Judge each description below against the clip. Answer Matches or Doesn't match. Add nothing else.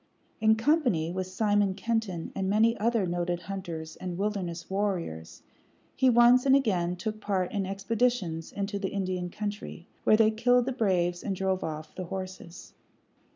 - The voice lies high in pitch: Matches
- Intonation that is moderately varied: Matches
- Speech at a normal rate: Matches